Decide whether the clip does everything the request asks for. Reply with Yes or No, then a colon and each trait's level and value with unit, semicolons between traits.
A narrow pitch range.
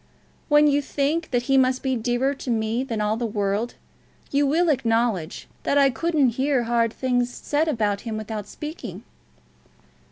No: average, 3.9 semitones